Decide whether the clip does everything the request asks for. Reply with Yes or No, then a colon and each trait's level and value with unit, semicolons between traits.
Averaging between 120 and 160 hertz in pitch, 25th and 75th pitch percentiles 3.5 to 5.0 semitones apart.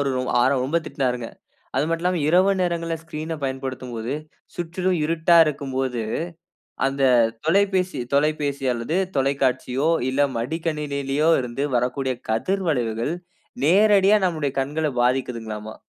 Yes: medium, 140 Hz; average, 4.4 semitones